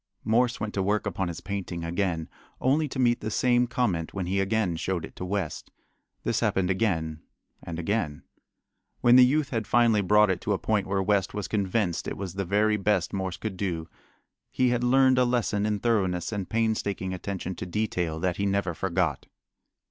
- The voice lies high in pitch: No, low, 100 Hz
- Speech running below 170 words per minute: No, average, 195 wpm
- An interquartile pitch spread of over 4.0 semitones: No, average, 3.5 semitones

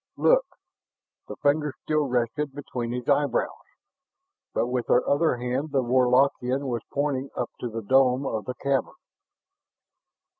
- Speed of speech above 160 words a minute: No, average, 140 wpm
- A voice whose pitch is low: Yes, low, 130 Hz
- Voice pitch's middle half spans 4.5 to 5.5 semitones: No, narrow, 2.5 semitones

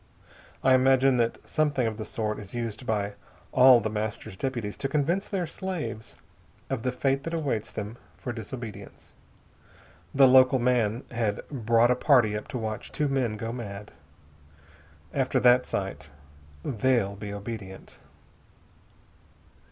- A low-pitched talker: Yes, low, 120 Hz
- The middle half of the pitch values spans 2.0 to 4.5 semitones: Yes, average, 3.7 semitones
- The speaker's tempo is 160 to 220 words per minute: No, average, 140 wpm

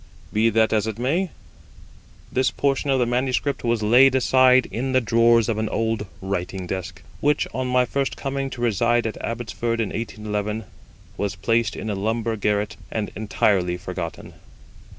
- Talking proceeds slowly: No, average, 165 wpm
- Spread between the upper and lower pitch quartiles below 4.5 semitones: Yes, average, 3.2 semitones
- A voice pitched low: Yes, low, 115 Hz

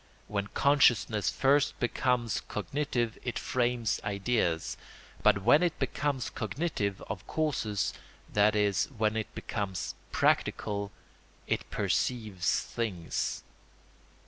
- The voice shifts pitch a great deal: No, average, 3.9 semitones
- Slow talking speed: Yes, slow, 100 wpm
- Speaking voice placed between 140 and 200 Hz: No, low, 110 Hz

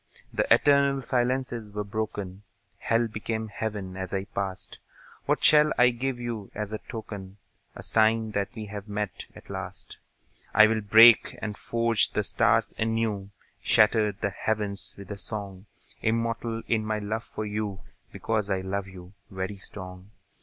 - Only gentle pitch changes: Yes, narrow, 2.3 semitones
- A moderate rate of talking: Yes, average, 155 wpm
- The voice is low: Yes, low, 105 Hz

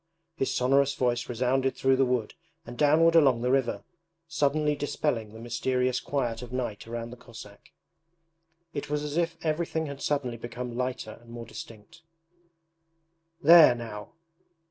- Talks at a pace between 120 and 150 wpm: Yes, average, 145 wpm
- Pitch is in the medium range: No, low, 125 Hz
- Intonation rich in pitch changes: No, average, 3.6 semitones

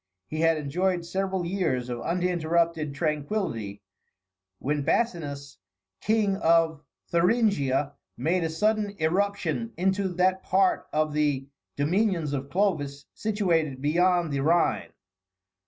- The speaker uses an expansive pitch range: No, average, 4.6 semitones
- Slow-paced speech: Yes, slow, 110 wpm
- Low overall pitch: No, medium, 165 Hz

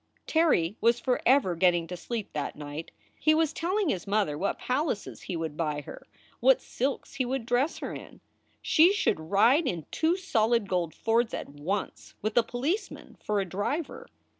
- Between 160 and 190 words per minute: Yes, average, 170 wpm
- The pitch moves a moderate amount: No, wide, 8.2 semitones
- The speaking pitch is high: Yes, high, 225 Hz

